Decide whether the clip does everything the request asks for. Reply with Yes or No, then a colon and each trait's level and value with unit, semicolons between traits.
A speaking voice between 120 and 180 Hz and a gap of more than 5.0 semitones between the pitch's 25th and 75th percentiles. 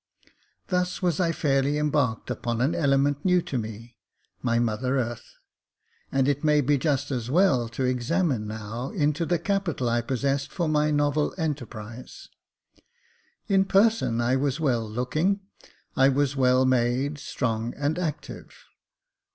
No: low, 135 Hz; average, 3.9 semitones